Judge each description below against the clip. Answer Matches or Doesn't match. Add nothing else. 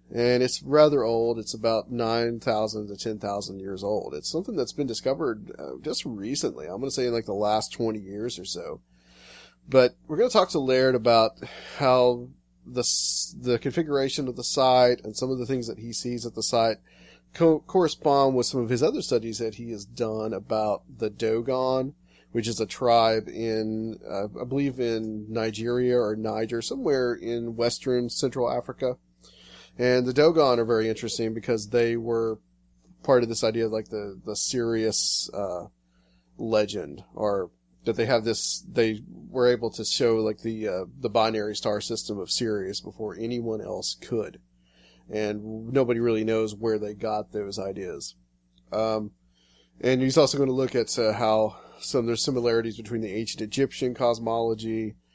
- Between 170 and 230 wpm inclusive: Matches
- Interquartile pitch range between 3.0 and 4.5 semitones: Doesn't match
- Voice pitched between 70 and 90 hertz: Doesn't match